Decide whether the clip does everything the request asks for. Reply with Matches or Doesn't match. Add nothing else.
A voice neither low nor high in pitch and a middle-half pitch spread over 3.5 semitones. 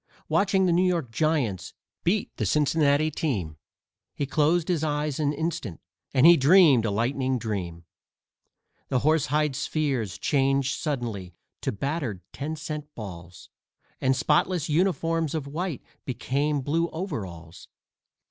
Matches